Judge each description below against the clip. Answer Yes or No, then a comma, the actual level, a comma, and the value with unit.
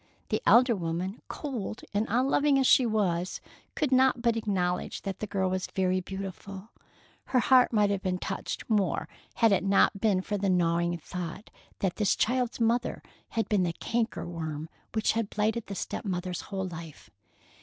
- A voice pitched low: No, high, 200 Hz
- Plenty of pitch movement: No, average, 4.0 semitones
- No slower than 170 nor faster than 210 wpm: Yes, average, 175 wpm